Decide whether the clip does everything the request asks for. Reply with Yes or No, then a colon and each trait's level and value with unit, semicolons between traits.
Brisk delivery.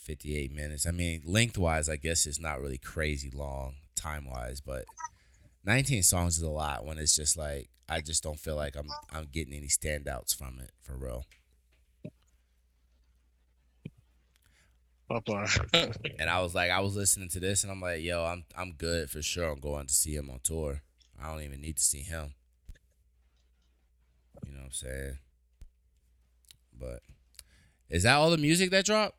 No: average, 175 wpm